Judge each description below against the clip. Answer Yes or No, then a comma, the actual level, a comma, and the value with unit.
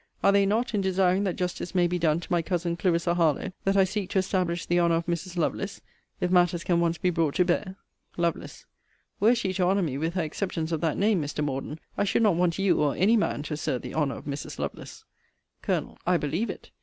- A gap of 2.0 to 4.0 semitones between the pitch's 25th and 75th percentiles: Yes, narrow, 2.5 semitones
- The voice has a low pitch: No, medium, 175 Hz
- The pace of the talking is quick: Yes, fast, 235 wpm